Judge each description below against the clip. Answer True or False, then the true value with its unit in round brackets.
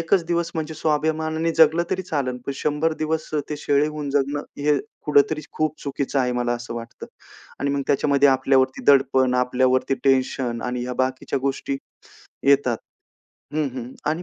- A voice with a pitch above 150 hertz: False (140 Hz)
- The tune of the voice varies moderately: True (3.0 semitones)